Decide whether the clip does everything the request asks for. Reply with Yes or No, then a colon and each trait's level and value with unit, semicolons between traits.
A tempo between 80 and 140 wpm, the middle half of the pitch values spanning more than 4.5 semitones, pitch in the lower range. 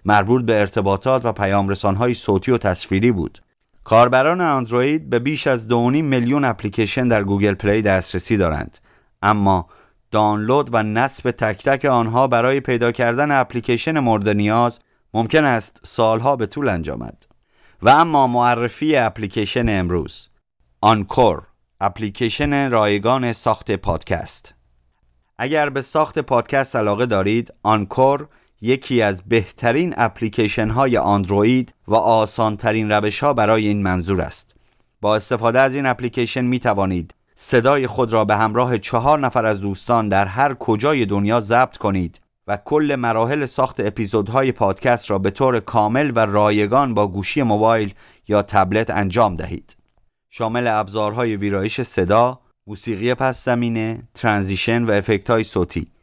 No: average, 135 wpm; average, 3.5 semitones; low, 115 Hz